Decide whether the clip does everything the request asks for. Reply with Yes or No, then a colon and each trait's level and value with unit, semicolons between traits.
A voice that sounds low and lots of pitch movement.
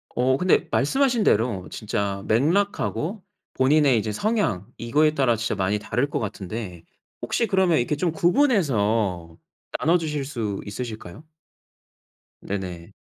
Yes: low, 125 Hz; wide, 7.8 semitones